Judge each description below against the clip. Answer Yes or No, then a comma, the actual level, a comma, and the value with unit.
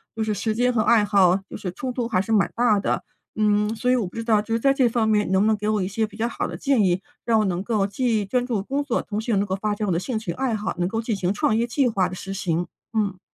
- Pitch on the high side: Yes, high, 215 Hz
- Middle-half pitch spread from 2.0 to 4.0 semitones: Yes, average, 2.9 semitones